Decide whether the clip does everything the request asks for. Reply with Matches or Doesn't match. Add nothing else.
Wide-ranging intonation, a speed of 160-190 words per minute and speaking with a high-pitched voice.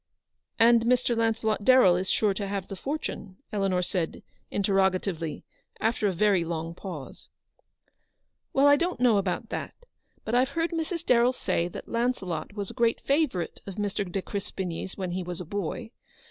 Doesn't match